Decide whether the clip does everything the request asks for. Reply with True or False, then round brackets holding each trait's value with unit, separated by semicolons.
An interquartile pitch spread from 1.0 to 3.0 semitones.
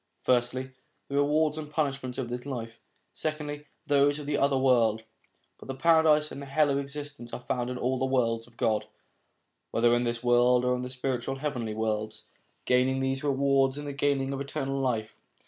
True (2.6 semitones)